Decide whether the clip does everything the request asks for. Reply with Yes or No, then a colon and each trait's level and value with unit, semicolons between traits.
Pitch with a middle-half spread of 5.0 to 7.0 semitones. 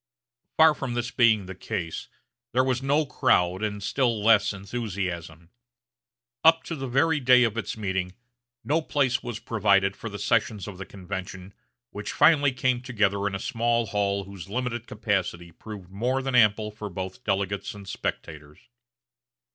No: average, 4.3 semitones